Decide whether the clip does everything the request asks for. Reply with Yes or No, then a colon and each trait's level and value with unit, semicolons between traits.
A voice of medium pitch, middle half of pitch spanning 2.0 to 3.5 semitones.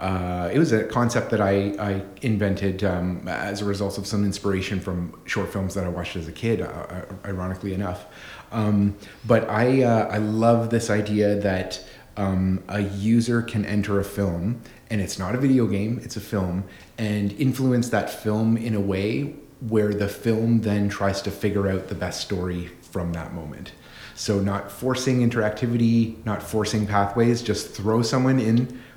No: low, 105 Hz; average, 2.8 semitones